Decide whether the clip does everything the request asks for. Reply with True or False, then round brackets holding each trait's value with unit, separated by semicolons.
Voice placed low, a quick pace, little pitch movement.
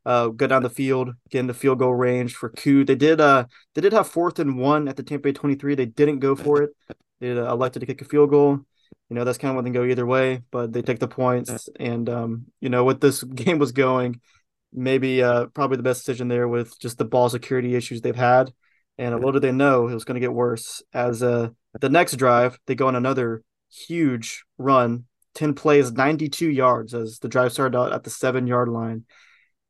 True (130 Hz; 235 wpm; 2.0 semitones)